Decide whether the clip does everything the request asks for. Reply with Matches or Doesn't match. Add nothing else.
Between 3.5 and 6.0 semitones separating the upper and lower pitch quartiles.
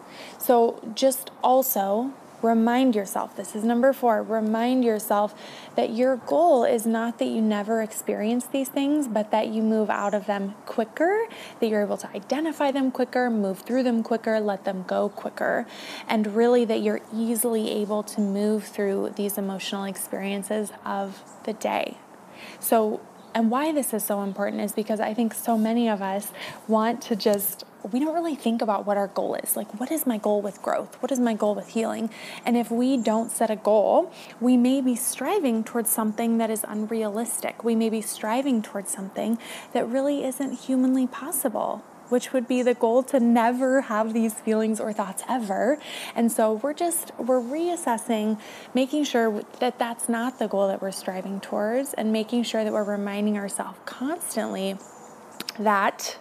Doesn't match